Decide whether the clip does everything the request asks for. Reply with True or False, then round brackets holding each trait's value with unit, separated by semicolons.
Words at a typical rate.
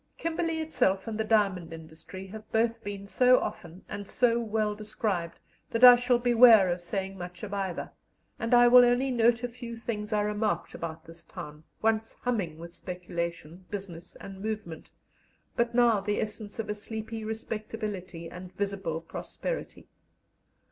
True (160 wpm)